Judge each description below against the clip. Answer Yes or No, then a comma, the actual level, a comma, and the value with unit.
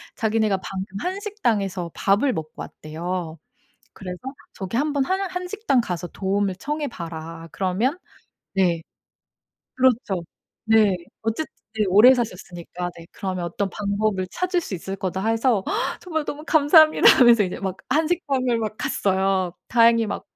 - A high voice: Yes, high, 210 Hz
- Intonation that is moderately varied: No, wide, 6.0 semitones